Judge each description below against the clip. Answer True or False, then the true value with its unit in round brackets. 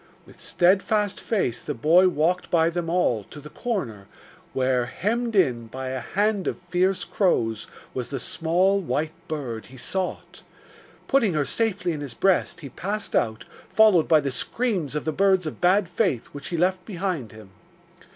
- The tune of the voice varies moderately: False (6.5 semitones)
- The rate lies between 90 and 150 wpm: False (170 wpm)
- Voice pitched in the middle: True (170 Hz)